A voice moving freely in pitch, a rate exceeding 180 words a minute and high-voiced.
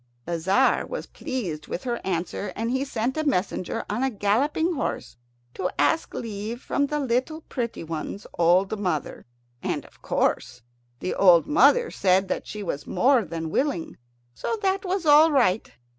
No: wide, 7.5 semitones; average, 165 wpm; high, 230 Hz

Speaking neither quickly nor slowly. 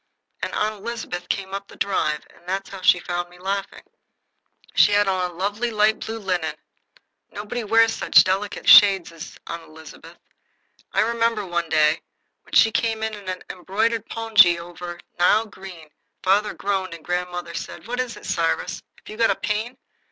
Yes: average, 175 wpm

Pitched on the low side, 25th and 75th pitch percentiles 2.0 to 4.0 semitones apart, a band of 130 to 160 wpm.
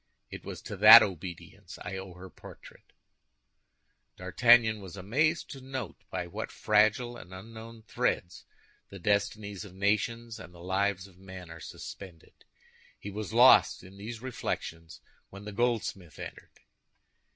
Yes: low, 100 Hz; average, 3.7 semitones; average, 140 wpm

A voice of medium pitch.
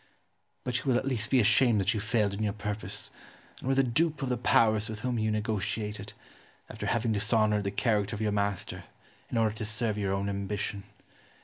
No: low, 110 Hz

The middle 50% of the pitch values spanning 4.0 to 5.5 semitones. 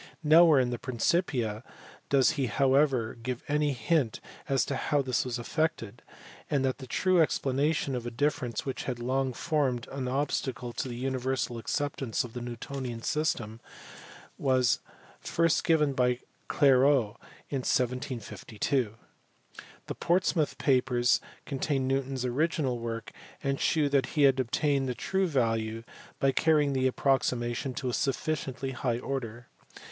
No: average, 2.9 semitones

